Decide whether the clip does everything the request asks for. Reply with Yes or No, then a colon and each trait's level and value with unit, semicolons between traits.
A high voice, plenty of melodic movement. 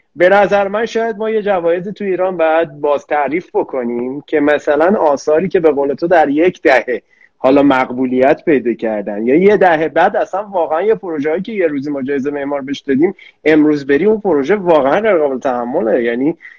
No: medium, 160 Hz; wide, 5.9 semitones